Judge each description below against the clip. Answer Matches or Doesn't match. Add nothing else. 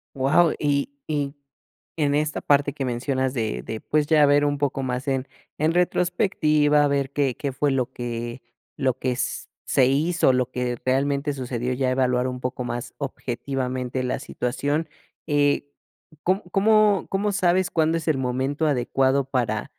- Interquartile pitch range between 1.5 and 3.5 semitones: Matches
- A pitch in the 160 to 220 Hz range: Doesn't match